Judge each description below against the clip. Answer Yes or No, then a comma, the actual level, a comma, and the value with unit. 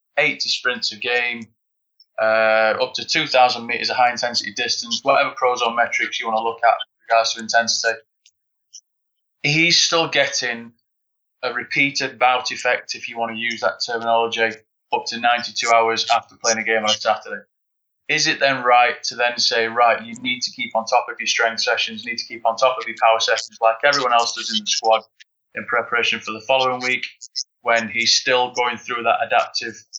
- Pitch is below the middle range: Yes, low, 120 Hz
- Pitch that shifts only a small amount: Yes, narrow, 2.2 semitones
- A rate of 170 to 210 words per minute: Yes, average, 200 wpm